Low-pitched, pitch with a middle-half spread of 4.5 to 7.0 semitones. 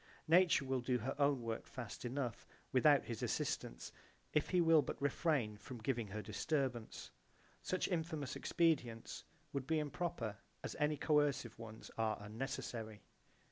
Yes: low, 130 Hz; average, 5.1 semitones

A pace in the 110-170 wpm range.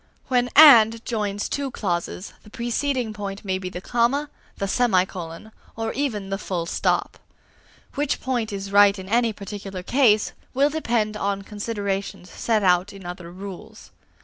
Yes: average, 150 wpm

